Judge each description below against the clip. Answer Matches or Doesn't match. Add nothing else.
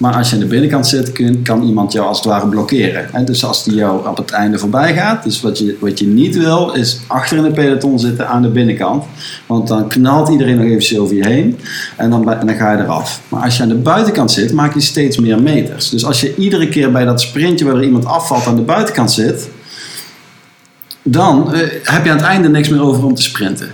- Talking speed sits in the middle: Doesn't match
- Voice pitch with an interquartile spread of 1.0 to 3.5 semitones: Doesn't match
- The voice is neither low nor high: Doesn't match